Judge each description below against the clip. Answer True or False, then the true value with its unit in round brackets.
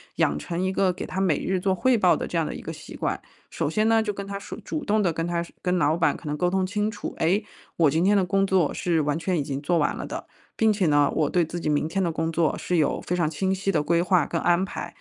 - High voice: False (180 Hz)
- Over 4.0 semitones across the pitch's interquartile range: False (3.3 semitones)